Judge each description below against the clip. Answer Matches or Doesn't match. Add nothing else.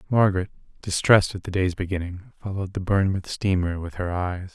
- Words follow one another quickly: Doesn't match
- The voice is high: Doesn't match